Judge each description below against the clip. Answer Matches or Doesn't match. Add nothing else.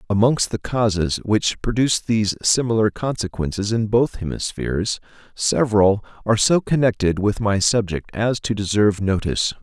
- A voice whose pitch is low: Matches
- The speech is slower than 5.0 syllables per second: Doesn't match